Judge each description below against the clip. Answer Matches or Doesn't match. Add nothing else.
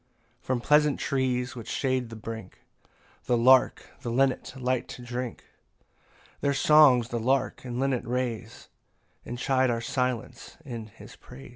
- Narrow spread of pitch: Matches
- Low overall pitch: Matches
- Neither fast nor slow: Matches